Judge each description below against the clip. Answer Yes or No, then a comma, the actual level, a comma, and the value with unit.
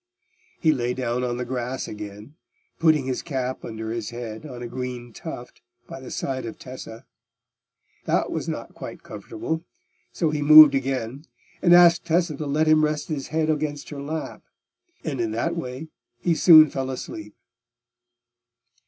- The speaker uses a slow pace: No, average, 160 wpm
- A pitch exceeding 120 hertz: Yes, low, 135 Hz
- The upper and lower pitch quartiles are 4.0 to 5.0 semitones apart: Yes, average, 4.3 semitones